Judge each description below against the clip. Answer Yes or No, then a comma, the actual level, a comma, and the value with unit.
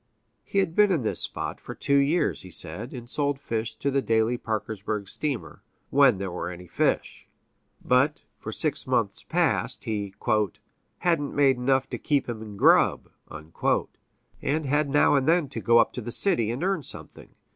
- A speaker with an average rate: Yes, average, 180 wpm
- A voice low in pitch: Yes, low, 130 Hz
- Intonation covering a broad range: No, average, 4.8 semitones